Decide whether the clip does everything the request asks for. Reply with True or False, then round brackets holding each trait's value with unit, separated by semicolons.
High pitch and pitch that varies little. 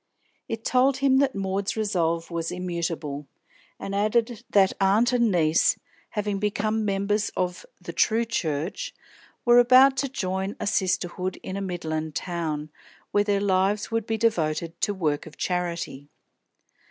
False (195 Hz; 4.5 semitones)